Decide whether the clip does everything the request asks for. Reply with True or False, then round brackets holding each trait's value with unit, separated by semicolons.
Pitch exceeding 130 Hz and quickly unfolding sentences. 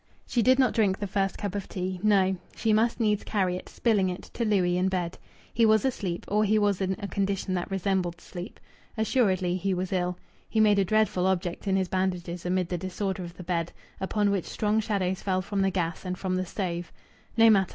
True (190 Hz; 220 wpm)